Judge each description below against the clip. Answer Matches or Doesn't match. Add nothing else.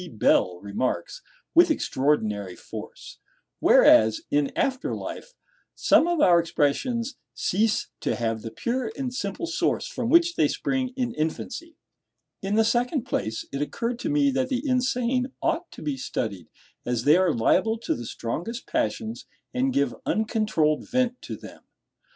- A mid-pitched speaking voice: Doesn't match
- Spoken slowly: Doesn't match